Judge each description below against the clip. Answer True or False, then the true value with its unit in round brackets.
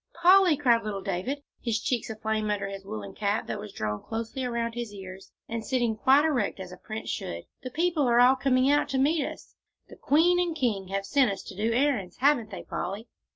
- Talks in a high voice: True (230 Hz)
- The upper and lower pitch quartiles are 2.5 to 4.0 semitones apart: False (5.4 semitones)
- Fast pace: True (220 wpm)